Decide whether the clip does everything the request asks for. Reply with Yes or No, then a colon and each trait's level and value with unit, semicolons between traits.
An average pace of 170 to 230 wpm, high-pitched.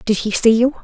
No: fast, 290 wpm; high, 225 Hz